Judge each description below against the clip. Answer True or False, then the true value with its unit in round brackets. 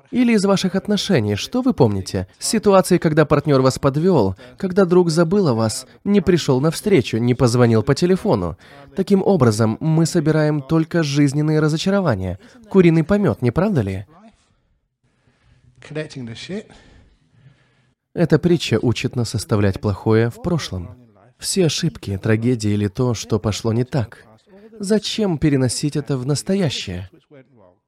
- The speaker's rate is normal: True (125 wpm)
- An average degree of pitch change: False (7.3 semitones)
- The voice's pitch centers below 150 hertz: True (140 Hz)